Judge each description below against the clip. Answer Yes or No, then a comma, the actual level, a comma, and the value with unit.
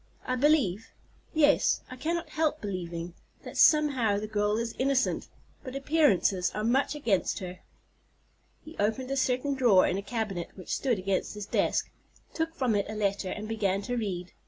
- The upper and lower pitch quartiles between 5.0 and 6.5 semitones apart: Yes, wide, 5.6 semitones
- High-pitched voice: Yes, high, 225 Hz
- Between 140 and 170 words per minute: Yes, average, 160 wpm